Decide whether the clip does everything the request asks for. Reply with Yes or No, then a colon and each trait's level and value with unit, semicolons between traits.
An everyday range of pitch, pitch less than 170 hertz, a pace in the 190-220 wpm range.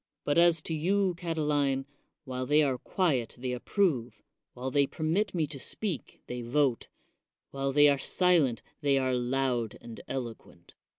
No: average, 4.1 semitones; medium, 140 Hz; average, 155 wpm